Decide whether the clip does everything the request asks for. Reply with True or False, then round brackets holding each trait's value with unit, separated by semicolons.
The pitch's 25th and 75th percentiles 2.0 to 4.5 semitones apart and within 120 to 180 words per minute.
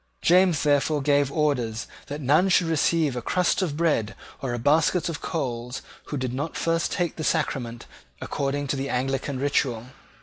True (3.9 semitones; 170 wpm)